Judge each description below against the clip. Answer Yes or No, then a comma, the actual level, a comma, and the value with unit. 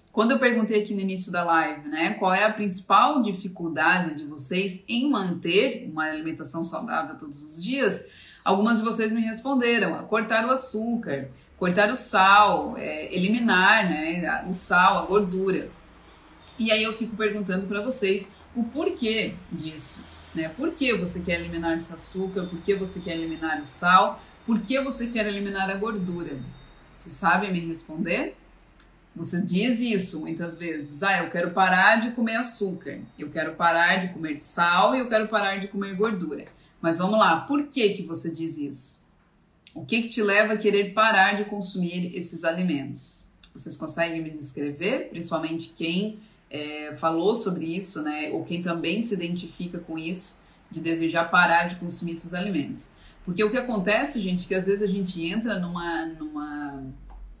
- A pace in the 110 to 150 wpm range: No, average, 170 wpm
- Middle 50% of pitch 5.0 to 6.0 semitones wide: No, average, 4.3 semitones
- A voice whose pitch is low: No, medium, 185 Hz